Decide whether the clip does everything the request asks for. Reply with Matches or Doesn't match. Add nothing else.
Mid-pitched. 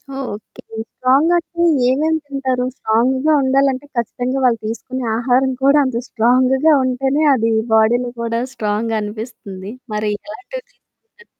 Doesn't match